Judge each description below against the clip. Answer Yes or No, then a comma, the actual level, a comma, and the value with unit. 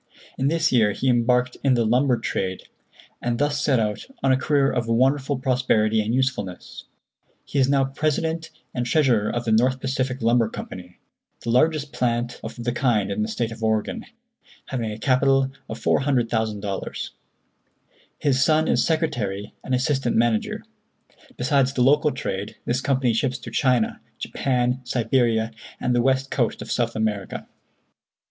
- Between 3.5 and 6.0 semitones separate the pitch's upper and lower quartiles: No, average, 3.1 semitones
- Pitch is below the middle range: Yes, low, 125 Hz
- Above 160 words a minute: No, average, 155 wpm